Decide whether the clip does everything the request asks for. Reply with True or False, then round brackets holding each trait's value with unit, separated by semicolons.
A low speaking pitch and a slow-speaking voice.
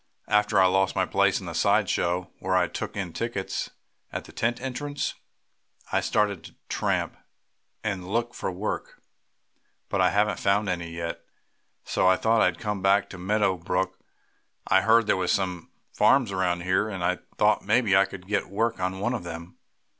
False (95 Hz; 185 wpm)